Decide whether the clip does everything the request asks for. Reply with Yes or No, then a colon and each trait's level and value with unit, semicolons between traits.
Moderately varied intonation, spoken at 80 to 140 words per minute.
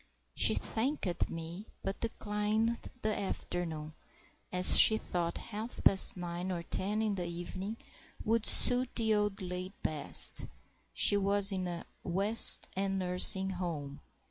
Yes: average, 3.3 semitones; slow, 135 wpm